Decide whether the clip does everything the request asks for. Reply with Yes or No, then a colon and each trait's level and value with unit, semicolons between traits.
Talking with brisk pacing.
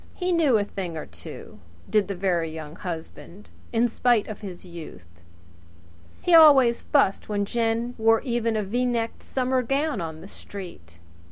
No: average, 165 wpm